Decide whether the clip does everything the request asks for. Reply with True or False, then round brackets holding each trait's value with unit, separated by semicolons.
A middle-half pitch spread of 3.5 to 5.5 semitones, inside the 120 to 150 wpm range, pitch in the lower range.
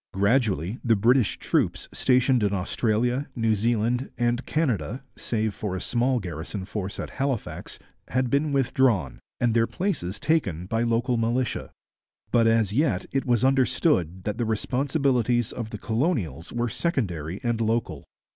True (4.0 semitones; 145 wpm; 115 Hz)